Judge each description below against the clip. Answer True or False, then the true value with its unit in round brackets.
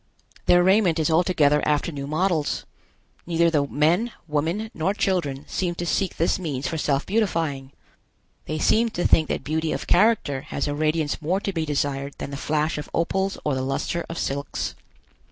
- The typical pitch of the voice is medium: True (160 Hz)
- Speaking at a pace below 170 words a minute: False (180 wpm)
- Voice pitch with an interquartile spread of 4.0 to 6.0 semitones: False (3.5 semitones)